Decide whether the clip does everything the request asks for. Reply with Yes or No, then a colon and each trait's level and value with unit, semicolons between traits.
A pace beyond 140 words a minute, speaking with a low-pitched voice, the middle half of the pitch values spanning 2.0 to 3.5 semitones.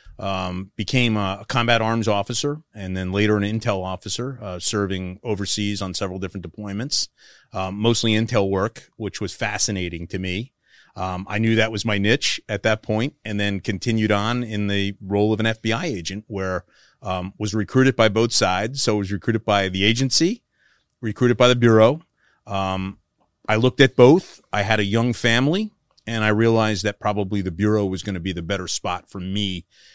Yes: average, 190 wpm; low, 105 Hz; average, 2.8 semitones